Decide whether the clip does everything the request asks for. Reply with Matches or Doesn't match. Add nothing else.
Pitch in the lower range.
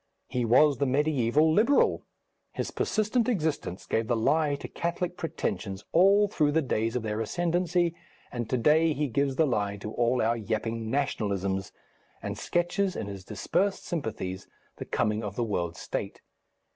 Matches